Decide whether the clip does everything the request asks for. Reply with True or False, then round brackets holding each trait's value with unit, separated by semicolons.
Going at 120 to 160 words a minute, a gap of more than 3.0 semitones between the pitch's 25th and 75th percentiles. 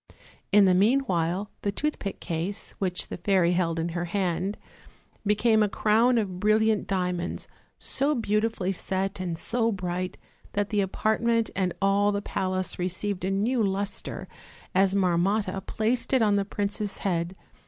False (150 wpm; 2.7 semitones)